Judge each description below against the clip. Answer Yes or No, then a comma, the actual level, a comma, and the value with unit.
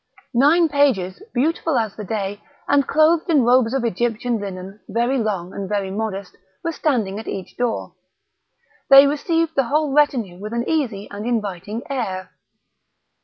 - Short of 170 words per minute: Yes, average, 155 wpm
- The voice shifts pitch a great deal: Yes, wide, 5.8 semitones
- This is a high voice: Yes, high, 235 Hz